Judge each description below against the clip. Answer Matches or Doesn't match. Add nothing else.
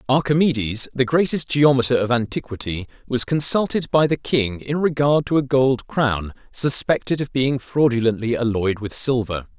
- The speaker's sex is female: Doesn't match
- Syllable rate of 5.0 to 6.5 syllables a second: Doesn't match